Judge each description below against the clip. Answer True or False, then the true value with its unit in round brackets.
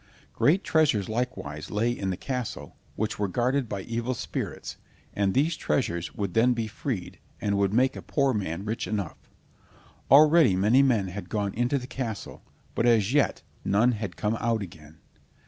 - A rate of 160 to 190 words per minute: True (170 wpm)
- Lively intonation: False (4.2 semitones)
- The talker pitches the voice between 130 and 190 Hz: False (110 Hz)